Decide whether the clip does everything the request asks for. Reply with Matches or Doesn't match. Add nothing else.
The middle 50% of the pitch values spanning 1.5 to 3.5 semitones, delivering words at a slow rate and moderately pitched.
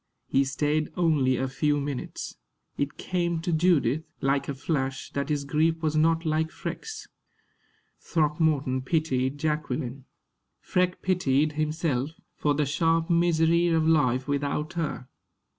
Matches